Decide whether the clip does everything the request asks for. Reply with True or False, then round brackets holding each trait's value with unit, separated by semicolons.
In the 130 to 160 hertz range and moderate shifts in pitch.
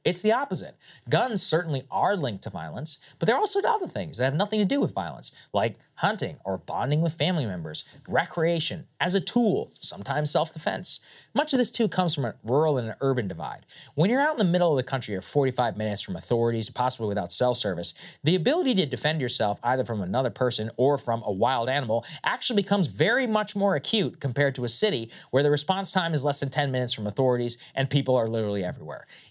False (140 Hz; 7.4 semitones)